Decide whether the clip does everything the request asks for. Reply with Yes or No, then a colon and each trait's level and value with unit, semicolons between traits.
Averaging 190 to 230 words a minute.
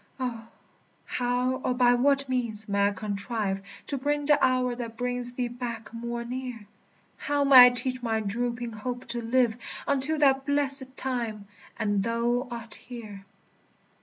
No: average, 155 wpm